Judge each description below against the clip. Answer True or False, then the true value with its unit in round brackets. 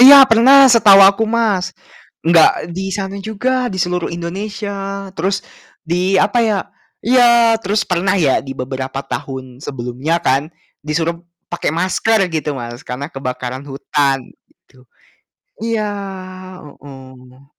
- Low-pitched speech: False (175 Hz)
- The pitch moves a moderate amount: False (7.2 semitones)